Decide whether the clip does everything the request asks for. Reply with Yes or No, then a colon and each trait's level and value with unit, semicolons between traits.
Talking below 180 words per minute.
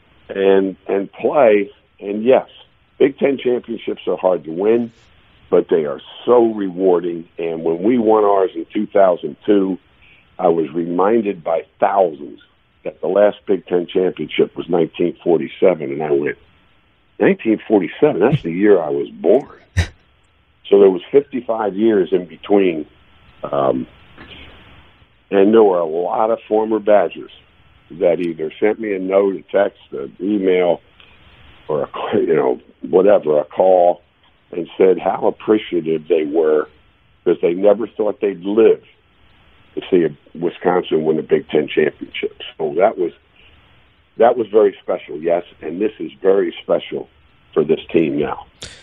Yes: average, 145 wpm